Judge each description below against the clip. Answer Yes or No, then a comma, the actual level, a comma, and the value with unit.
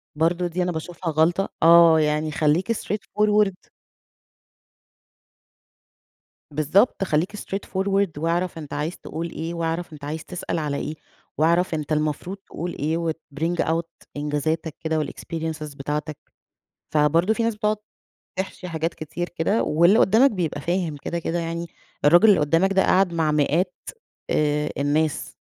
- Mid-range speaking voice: Yes, medium, 165 Hz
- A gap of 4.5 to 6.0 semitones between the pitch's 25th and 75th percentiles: No, average, 2.9 semitones